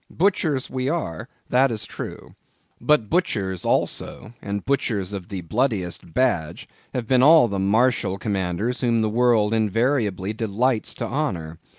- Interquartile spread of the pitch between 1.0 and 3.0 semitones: No, average, 4.9 semitones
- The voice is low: Yes, low, 110 Hz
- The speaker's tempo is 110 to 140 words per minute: Yes, slow, 135 wpm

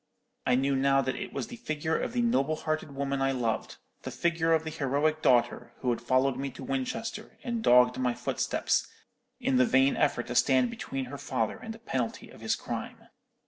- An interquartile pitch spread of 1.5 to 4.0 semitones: Yes, average, 3.6 semitones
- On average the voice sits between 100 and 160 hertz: Yes, low, 135 Hz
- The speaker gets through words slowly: No, average, 200 wpm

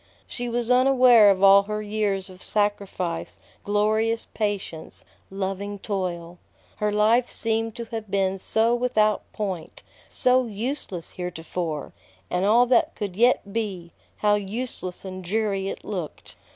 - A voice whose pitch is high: Yes, high, 205 Hz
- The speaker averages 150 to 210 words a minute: No, slow, 135 wpm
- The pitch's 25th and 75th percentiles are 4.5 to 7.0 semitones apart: No, average, 3.0 semitones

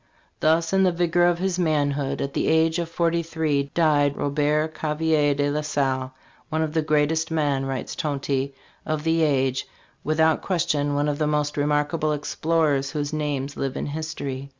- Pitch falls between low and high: Yes, medium, 150 Hz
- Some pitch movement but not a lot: No, narrow, 2.1 semitones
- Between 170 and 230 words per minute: Yes, average, 175 wpm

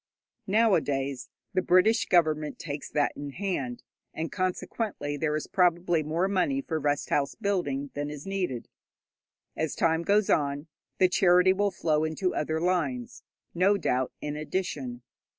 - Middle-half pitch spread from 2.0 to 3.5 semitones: No, average, 4.2 semitones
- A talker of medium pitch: Yes, medium, 160 Hz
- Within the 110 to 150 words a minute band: Yes, average, 145 wpm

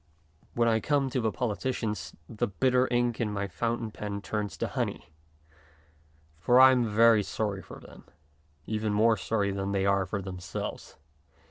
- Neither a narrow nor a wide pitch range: Yes, average, 3.1 semitones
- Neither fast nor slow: Yes, average, 160 wpm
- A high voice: No, low, 110 Hz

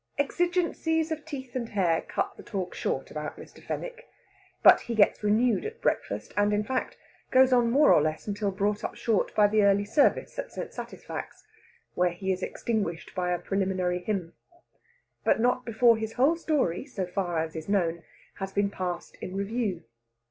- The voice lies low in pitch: No, high, 205 Hz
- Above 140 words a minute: Yes, average, 180 wpm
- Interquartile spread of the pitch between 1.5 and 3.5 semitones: No, wide, 5.4 semitones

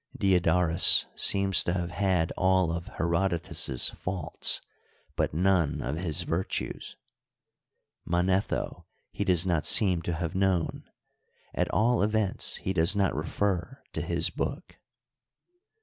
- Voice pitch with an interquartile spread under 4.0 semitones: Yes, narrow, 2.4 semitones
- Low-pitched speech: Yes, very low, 90 Hz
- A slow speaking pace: Yes, slow, 120 wpm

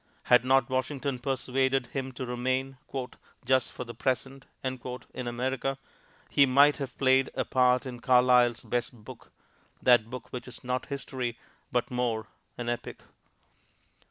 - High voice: No, low, 125 Hz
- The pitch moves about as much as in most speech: No, narrow, 1.3 semitones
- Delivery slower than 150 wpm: Yes, average, 140 wpm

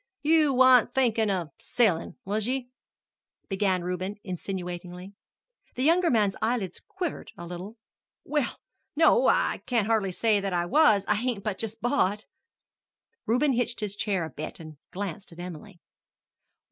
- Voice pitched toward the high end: Yes, high, 210 Hz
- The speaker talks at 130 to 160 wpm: Yes, average, 145 wpm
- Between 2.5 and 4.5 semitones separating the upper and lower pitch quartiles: No, average, 5.2 semitones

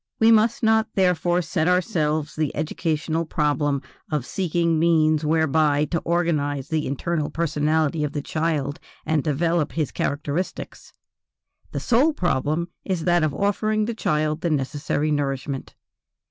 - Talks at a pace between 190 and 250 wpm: No, slow, 135 wpm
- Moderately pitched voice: Yes, medium, 155 Hz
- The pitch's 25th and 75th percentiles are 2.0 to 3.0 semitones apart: Yes, average, 2.7 semitones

